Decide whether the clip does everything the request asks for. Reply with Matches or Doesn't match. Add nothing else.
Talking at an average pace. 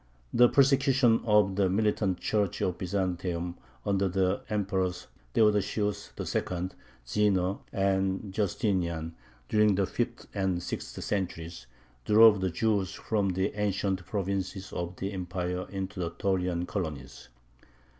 Doesn't match